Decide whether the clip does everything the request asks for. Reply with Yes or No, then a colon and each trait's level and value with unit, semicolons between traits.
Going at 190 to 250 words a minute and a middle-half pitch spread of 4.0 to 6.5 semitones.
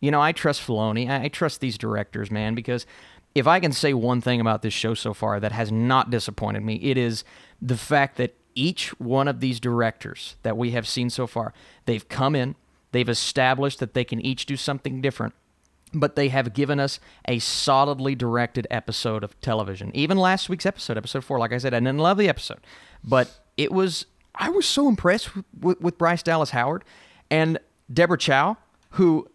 Yes: average, 195 wpm; average, 4.3 semitones